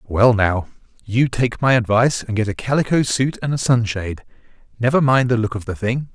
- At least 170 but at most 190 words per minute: No, fast, 205 wpm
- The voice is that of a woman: No, male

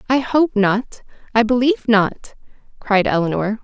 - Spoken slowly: Yes, slow, 130 wpm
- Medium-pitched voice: No, high, 230 Hz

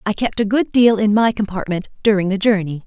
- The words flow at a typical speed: No, fast, 230 wpm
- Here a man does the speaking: No, female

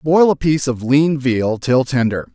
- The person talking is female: No, male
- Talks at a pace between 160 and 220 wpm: Yes, fast, 205 wpm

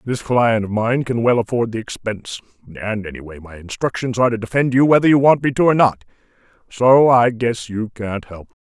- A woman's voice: No, male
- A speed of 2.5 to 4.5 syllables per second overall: No, 5.9 syllables/s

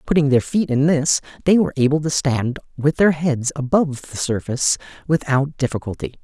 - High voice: No, medium, 140 Hz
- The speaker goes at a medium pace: Yes, average, 175 wpm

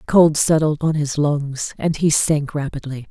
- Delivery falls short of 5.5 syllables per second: Yes, 4.6 syllables/s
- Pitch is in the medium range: Yes, medium, 150 Hz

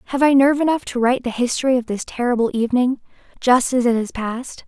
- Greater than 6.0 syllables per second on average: Yes, 6.8 syllables/s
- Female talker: Yes, female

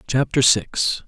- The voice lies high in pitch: No, low, 120 Hz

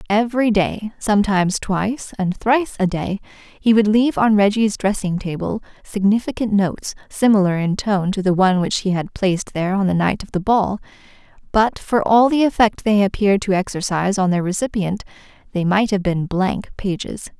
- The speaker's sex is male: No, female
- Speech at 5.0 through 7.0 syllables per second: Yes, 5.3 syllables/s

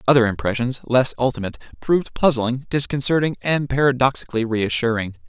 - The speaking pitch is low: Yes, low, 125 Hz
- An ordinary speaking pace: No, slow, 115 wpm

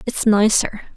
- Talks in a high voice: Yes, high, 215 Hz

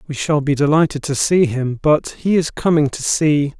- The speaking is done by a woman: No, male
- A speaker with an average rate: No, fast, 215 wpm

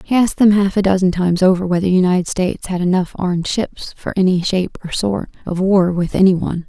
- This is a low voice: No, medium, 185 Hz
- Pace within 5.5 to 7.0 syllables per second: Yes, 6.3 syllables/s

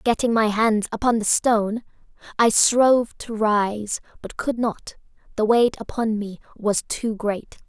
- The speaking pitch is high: Yes, high, 220 Hz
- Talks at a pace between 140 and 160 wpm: Yes, average, 155 wpm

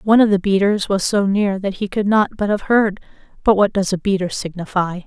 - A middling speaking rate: No, fast, 225 wpm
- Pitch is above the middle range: Yes, high, 200 Hz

